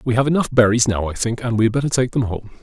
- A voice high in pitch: No, low, 120 Hz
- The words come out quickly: Yes, fast, 320 wpm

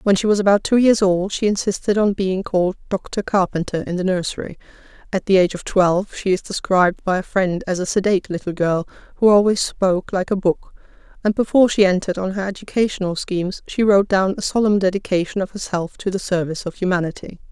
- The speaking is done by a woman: Yes, female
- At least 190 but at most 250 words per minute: Yes, fast, 205 wpm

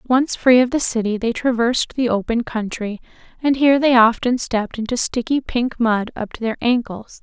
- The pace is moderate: Yes, average, 190 wpm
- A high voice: Yes, high, 240 Hz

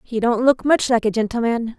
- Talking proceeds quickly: Yes, fast, 235 wpm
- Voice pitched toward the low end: No, high, 235 Hz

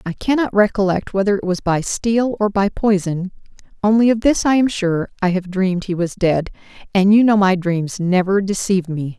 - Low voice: No, high, 195 Hz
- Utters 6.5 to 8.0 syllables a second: No, 5.1 syllables/s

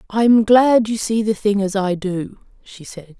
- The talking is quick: Yes, fast, 225 wpm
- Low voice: No, high, 205 Hz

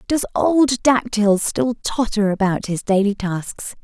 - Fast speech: No, average, 140 wpm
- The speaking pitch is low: No, high, 220 Hz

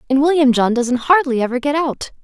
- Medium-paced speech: No, fast, 215 wpm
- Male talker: No, female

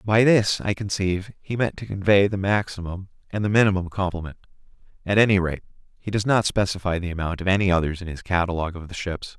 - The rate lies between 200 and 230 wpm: Yes, fast, 205 wpm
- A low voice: Yes, very low, 95 Hz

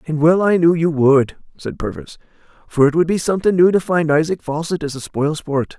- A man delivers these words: Yes, male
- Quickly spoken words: Yes, fast, 230 wpm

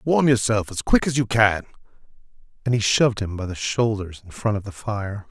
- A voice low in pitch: Yes, low, 110 Hz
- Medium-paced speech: No, fast, 215 wpm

